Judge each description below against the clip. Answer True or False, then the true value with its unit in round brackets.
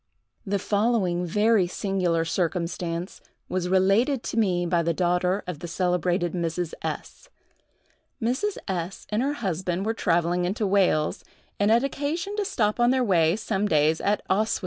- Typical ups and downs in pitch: True (4.1 semitones)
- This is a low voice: False (190 Hz)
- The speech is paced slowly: False (155 wpm)